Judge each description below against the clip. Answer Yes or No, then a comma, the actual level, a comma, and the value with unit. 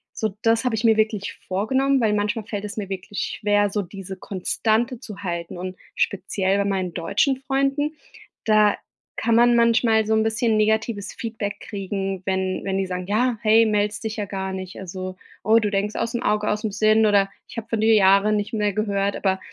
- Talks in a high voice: Yes, high, 210 Hz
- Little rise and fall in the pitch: Yes, narrow, 2.3 semitones